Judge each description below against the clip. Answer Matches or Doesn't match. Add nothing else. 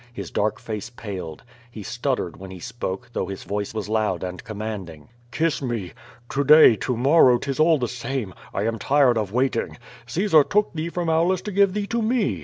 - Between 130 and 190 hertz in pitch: Doesn't match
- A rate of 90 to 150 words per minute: Doesn't match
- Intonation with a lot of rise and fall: Matches